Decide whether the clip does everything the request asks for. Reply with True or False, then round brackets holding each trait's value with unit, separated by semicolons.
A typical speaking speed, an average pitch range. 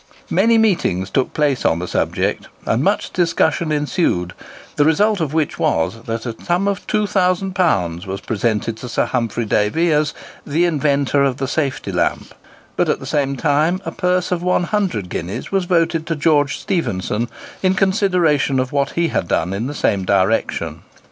False (170 wpm; 7.5 semitones)